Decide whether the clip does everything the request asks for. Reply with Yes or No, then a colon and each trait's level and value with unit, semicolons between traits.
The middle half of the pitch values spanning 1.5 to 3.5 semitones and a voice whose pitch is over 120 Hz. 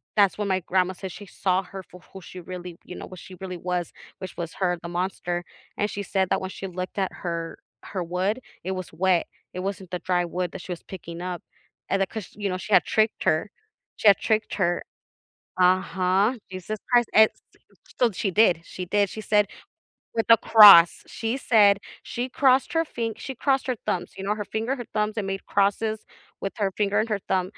Yes: average, 2.8 semitones; high, 190 Hz